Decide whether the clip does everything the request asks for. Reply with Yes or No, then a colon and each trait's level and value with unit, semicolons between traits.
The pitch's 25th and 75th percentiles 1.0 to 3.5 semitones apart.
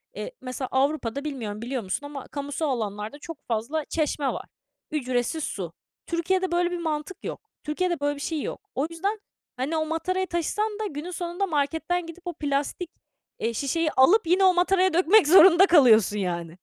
No: average, 5.1 semitones